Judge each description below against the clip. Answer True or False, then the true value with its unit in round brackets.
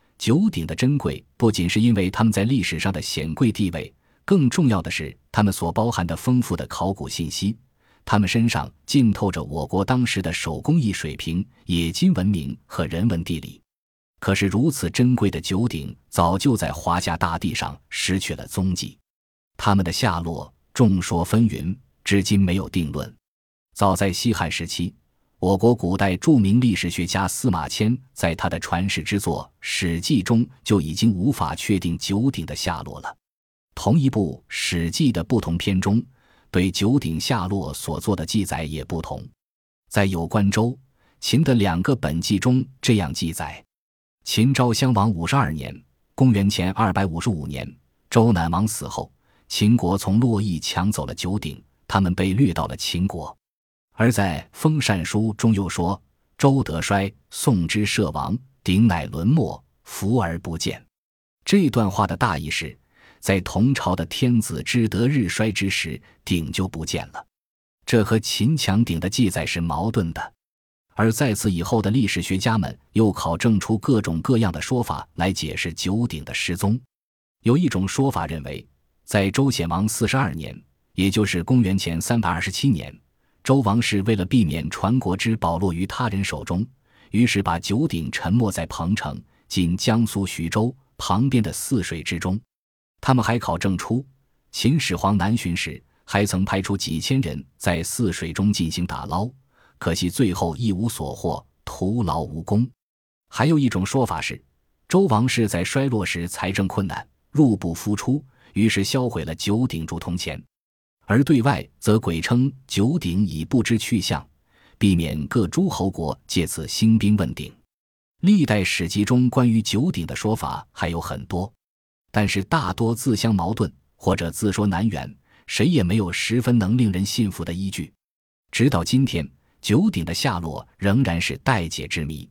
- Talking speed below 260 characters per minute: True (240 characters per minute)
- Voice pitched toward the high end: False (100 Hz)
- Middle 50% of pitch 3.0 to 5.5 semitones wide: True (5.1 semitones)